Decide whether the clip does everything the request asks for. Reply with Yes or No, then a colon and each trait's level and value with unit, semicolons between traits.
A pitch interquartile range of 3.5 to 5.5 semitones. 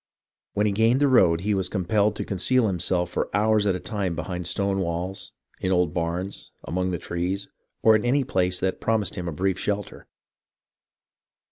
No: average, 2.8 semitones